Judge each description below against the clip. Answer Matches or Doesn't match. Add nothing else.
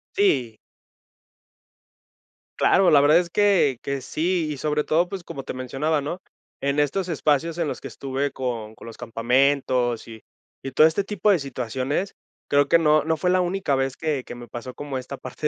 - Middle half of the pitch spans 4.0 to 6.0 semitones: Matches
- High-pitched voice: Doesn't match